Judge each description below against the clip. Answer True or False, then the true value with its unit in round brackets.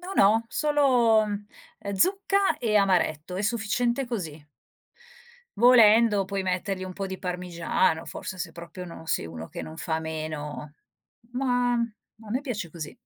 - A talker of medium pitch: False (200 Hz)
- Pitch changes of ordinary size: False (5.8 semitones)